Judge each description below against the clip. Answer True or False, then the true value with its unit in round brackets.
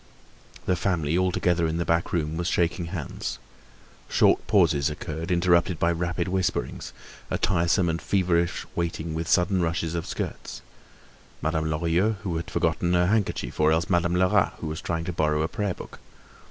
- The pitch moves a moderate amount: False (1.5 semitones)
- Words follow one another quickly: False (165 wpm)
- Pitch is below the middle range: True (85 Hz)